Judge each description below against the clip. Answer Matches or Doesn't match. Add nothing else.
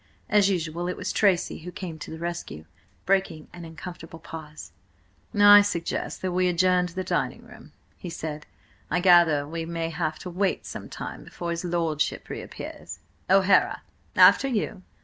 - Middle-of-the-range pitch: Matches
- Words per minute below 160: Doesn't match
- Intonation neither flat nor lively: Doesn't match